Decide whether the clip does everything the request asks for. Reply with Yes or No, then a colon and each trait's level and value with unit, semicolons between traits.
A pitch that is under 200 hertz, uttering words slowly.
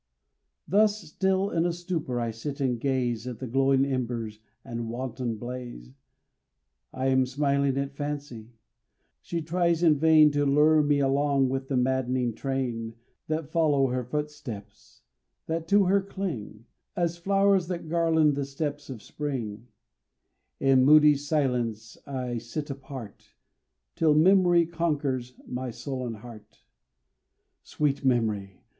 Yes: low, 135 Hz; slow, 130 wpm